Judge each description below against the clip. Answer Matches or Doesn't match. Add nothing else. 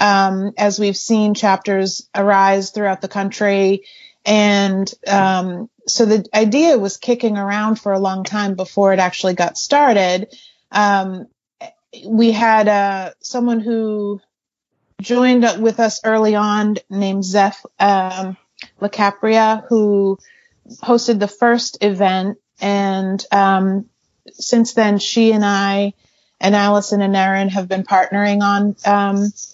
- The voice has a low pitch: Doesn't match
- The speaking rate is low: Matches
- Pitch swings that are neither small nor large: Doesn't match